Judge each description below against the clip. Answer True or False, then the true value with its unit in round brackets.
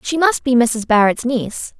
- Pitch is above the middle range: True (240 Hz)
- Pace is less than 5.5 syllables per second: True (4.8 syllables/s)